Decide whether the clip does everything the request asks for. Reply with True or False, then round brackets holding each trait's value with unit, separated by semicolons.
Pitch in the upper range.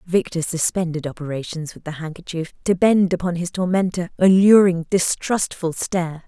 False (175 Hz)